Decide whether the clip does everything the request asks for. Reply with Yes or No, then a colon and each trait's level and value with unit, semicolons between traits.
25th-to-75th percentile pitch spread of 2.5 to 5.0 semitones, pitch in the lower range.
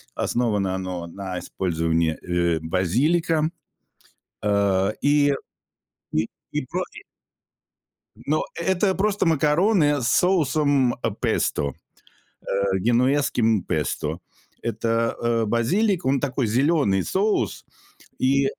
No: wide, 7.6 semitones; low, 120 Hz